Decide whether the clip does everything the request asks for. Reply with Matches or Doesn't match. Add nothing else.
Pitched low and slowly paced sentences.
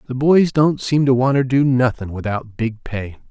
Doesn't match